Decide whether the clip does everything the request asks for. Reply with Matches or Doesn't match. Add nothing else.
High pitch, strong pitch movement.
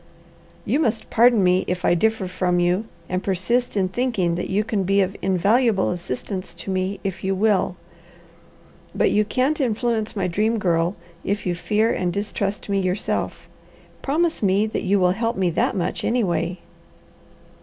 Doesn't match